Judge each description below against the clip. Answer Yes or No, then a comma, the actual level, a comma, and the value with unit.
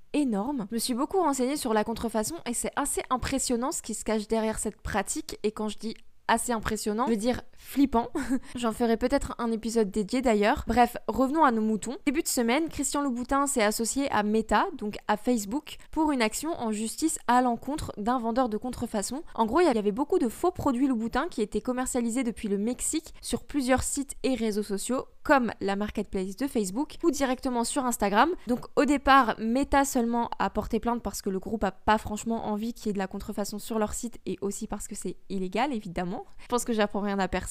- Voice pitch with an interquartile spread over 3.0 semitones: Yes, average, 3.9 semitones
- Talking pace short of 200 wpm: No, average, 215 wpm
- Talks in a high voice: Yes, high, 235 Hz